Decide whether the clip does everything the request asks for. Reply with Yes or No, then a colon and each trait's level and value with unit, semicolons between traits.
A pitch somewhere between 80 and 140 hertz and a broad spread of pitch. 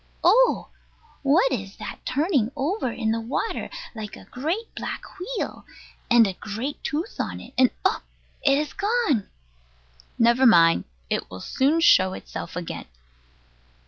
No: very high, 260 Hz; wide, 6.7 semitones